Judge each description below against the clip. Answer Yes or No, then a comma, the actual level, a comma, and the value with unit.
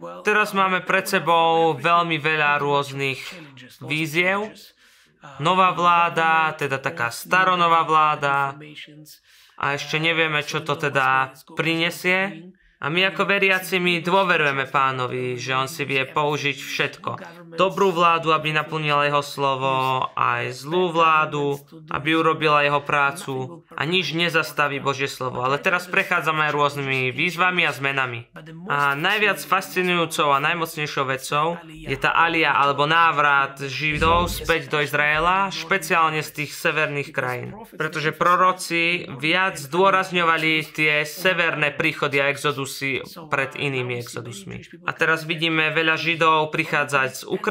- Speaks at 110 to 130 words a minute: Yes, average, 125 wpm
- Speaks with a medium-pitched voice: Yes, medium, 155 Hz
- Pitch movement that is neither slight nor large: Yes, average, 3.3 semitones